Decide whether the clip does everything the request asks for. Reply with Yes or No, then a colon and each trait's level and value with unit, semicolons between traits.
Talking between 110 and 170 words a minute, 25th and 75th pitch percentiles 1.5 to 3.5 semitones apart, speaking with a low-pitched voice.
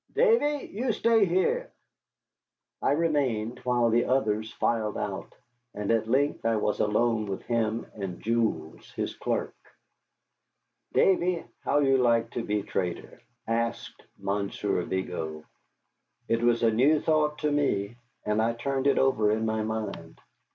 No: average, 140 wpm; average, 4.9 semitones; low, 115 Hz